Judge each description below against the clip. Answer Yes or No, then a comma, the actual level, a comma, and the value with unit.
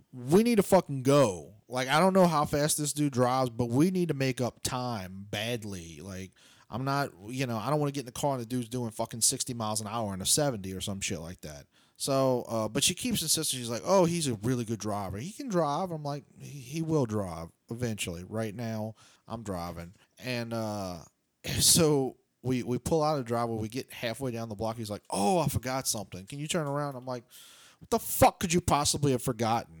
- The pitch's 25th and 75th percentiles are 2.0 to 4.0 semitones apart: No, average, 5.1 semitones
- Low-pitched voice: Yes, low, 125 Hz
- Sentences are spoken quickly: Yes, fast, 235 wpm